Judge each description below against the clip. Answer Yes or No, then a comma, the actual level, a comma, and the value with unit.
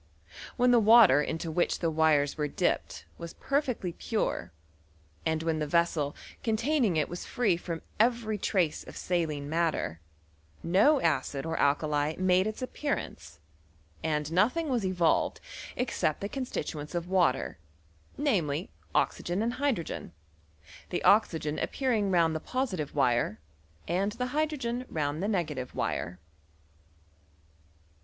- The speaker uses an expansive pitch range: Yes, wide, 6.8 semitones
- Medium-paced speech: No, slow, 130 wpm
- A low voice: No, medium, 175 Hz